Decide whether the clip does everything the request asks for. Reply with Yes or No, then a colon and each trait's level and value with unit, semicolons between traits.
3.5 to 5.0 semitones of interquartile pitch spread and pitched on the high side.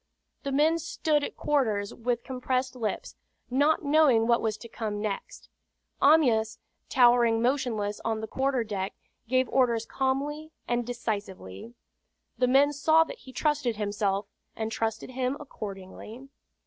Yes: average, 3.9 semitones; high, 245 Hz